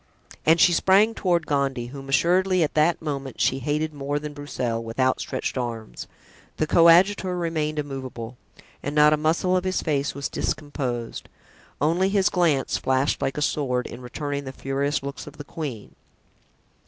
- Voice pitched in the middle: Yes, medium, 145 Hz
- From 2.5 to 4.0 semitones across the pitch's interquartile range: Yes, average, 3.7 semitones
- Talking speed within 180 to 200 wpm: No, average, 165 wpm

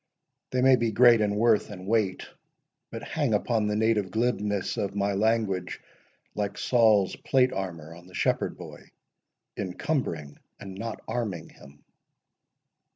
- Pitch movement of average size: Yes, average, 3.5 semitones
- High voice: No, low, 105 Hz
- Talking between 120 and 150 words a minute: Yes, average, 140 wpm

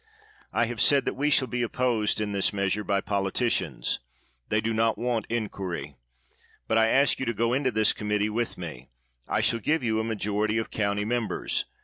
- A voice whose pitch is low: Yes, low, 110 Hz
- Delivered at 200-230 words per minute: Yes, fast, 205 wpm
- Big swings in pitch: No, narrow, 2.5 semitones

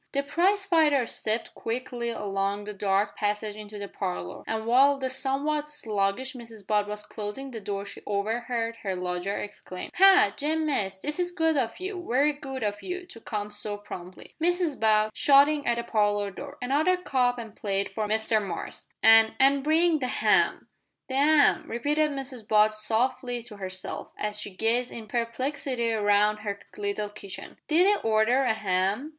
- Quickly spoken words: No, average, 175 wpm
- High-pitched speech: Yes, high, 230 Hz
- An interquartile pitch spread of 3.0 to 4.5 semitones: No, average, 5.2 semitones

